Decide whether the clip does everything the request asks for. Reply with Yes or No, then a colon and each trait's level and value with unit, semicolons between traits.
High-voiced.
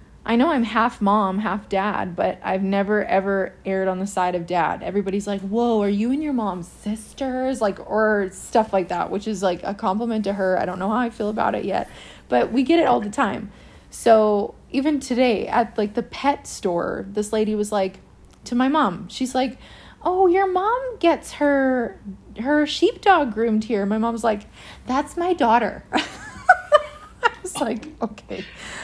Yes: high, 225 Hz